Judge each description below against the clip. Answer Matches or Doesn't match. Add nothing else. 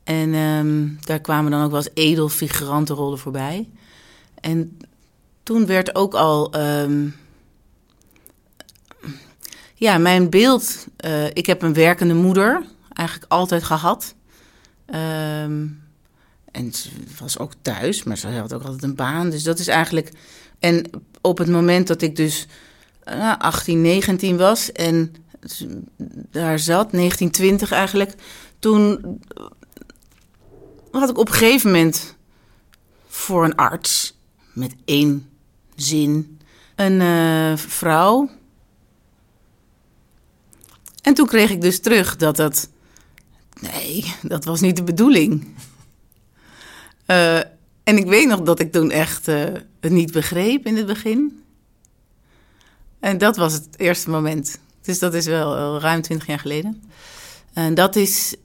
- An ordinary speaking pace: Doesn't match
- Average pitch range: Matches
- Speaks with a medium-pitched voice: Matches